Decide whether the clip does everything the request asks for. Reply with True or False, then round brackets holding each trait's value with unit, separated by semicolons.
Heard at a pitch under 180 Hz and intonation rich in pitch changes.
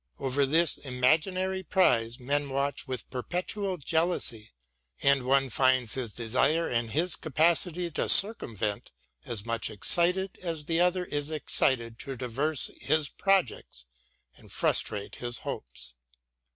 True (140 Hz; 5.8 semitones)